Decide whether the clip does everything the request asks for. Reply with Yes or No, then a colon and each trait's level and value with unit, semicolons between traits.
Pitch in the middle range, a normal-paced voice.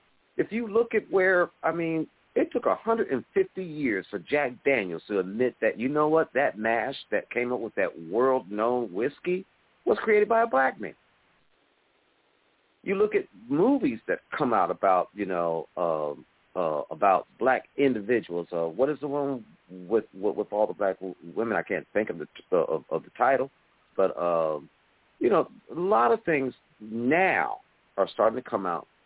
No: low, 130 Hz; average, 175 wpm